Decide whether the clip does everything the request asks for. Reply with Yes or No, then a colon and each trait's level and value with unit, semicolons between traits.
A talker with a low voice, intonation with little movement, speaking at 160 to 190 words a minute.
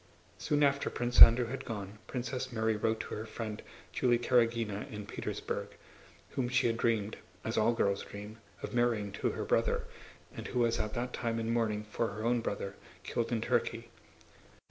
Yes: low, 115 Hz; narrow, 2.1 semitones; average, 180 wpm